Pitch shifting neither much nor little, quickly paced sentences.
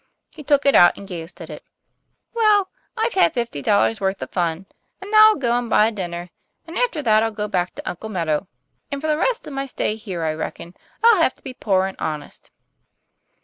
No: wide, 9.0 semitones; fast, 225 wpm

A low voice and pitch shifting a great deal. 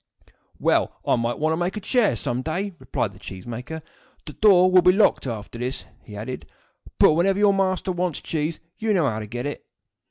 No: medium, 160 Hz; wide, 7.4 semitones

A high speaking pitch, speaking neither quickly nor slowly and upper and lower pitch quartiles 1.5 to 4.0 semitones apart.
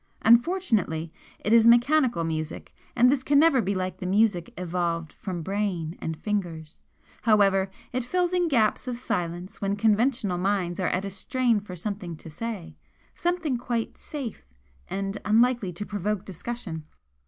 No: high, 205 Hz; average, 155 wpm; average, 5.1 semitones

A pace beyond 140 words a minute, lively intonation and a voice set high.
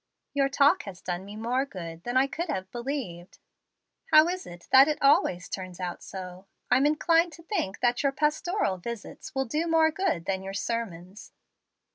Yes: average, 180 wpm; wide, 8.2 semitones; high, 245 Hz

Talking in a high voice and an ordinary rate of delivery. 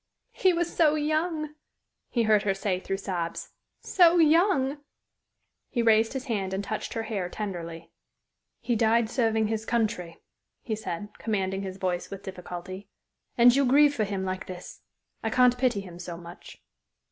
Yes: high, 220 Hz; average, 160 wpm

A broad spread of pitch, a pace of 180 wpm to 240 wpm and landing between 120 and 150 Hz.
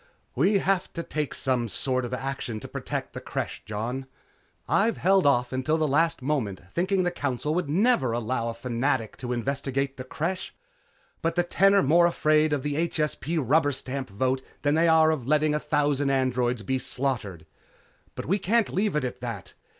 No: average, 4.3 semitones; average, 185 wpm; medium, 140 Hz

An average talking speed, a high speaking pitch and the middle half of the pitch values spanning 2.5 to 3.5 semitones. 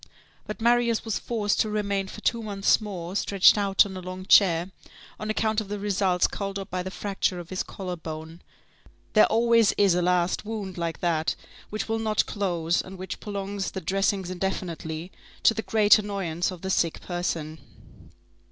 Yes: average, 180 wpm; high, 195 Hz; average, 2.8 semitones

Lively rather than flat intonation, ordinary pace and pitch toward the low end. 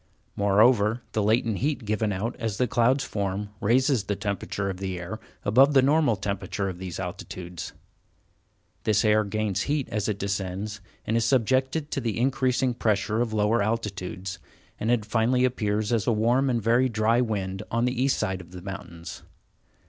No: average, 3.5 semitones; average, 175 wpm; low, 110 Hz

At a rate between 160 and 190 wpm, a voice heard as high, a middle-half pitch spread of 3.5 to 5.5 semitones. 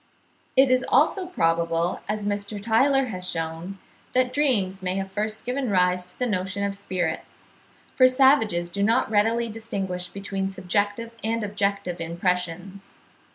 No: average, 145 wpm; high, 200 Hz; average, 4.0 semitones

